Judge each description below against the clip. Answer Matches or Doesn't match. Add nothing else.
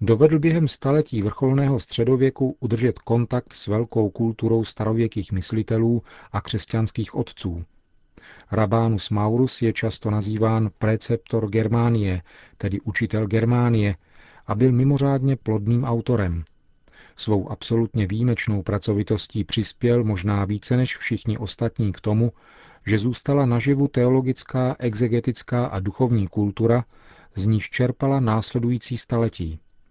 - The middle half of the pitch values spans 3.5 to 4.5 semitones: Doesn't match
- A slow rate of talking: Matches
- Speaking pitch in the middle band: Doesn't match